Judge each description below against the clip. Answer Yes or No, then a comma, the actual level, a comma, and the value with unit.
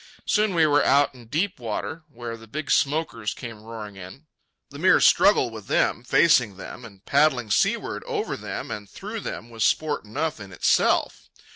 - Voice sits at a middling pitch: No, low, 120 Hz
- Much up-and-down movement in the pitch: Yes, wide, 6.0 semitones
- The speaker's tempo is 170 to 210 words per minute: Yes, average, 175 wpm